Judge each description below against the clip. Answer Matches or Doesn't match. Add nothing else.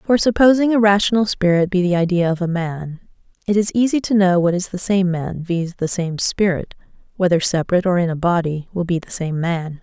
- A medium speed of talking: Doesn't match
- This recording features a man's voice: Doesn't match